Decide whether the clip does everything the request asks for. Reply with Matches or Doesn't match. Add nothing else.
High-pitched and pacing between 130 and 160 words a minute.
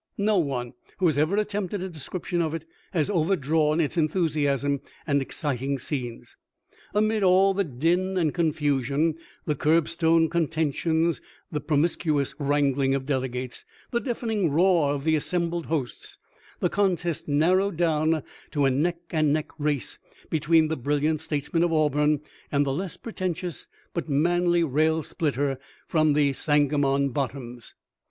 Doesn't match